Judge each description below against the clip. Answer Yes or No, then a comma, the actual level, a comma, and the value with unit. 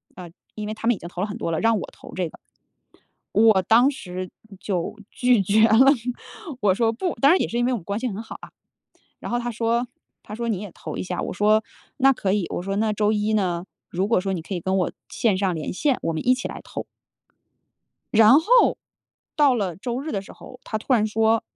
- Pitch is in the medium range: No, high, 215 Hz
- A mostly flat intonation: No, average, 4.0 semitones